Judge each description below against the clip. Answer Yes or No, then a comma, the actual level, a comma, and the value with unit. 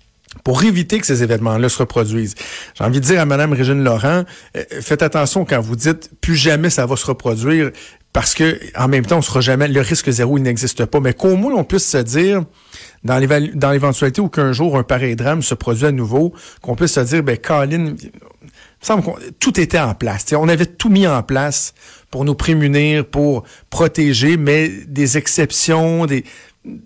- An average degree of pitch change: Yes, average, 4.1 semitones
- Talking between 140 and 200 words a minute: Yes, average, 195 wpm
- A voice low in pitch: No, medium, 145 Hz